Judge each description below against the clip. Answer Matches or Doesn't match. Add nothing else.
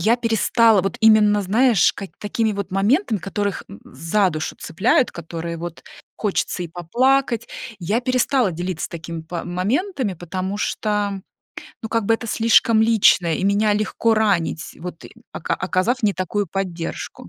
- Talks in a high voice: Matches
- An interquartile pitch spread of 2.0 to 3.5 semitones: Doesn't match